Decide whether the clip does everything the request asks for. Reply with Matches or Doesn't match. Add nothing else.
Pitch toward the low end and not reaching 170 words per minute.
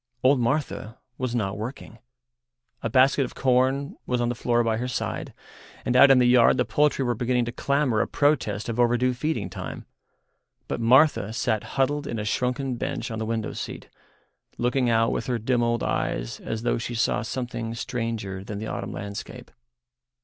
Doesn't match